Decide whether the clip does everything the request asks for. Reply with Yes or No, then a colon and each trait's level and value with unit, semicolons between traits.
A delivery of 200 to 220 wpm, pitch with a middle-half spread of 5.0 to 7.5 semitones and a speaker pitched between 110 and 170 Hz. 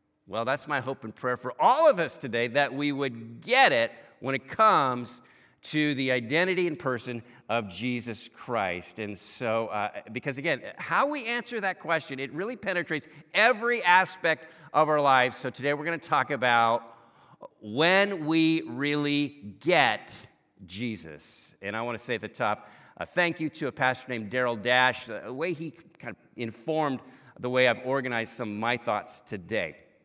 No: average, 180 wpm; wide, 5.4 semitones; low, 135 Hz